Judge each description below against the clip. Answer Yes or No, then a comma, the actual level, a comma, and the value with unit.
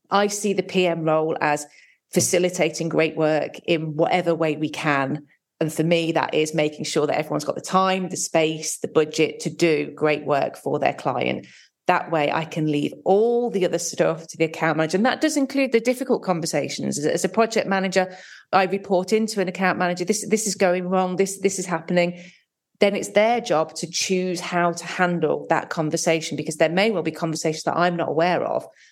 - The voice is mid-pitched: Yes, medium, 175 Hz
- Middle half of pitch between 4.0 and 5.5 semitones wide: No, average, 3.0 semitones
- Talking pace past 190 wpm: Yes, fast, 205 wpm